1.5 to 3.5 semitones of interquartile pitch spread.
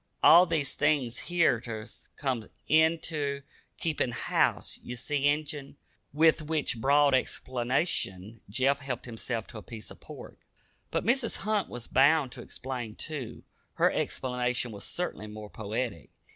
No: average, 4.7 semitones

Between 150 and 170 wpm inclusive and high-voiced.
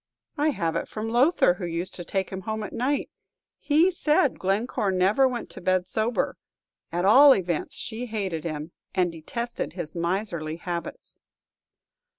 Yes: average, 160 wpm; high, 195 Hz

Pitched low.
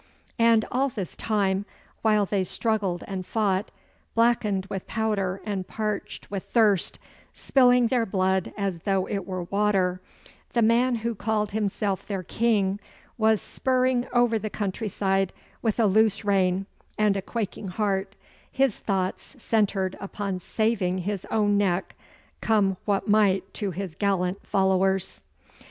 No: high, 205 Hz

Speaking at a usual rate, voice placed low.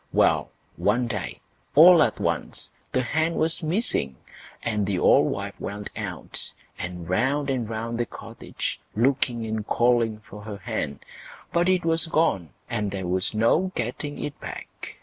Yes: average, 150 wpm; low, 115 Hz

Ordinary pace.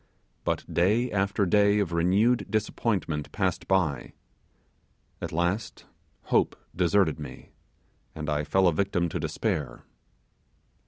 No: slow, 115 wpm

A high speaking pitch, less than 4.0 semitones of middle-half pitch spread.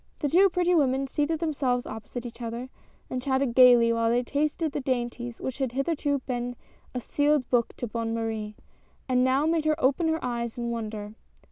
Yes: very high, 255 Hz; average, 3.6 semitones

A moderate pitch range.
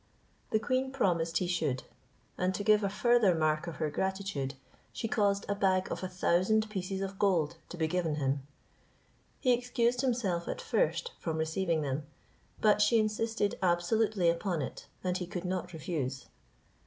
Yes: average, 4.2 semitones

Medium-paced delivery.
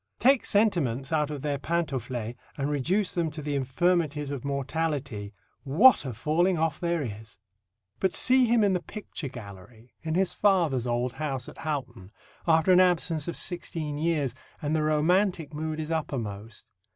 Yes: average, 165 wpm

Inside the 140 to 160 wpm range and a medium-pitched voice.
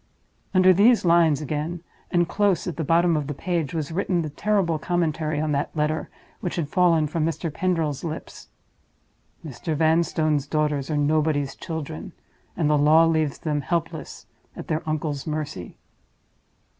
Yes: average, 155 wpm; medium, 155 Hz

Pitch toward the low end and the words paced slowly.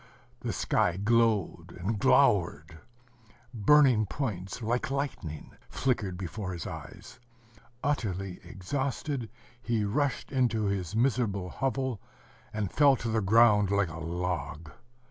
Yes: low, 105 Hz; slow, 115 wpm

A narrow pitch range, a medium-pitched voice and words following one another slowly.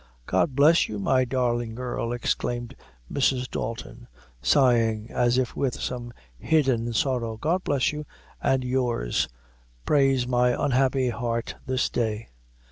No: narrow, 2.1 semitones; low, 125 Hz; slow, 125 wpm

